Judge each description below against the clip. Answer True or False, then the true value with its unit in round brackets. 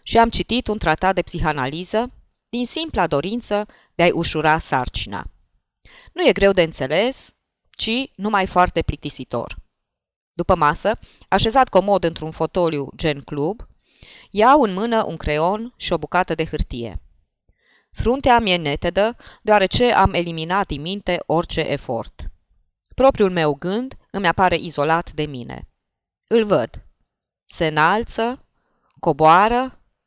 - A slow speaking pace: False (130 wpm)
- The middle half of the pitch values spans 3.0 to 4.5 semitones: False (5.6 semitones)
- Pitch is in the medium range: True (175 Hz)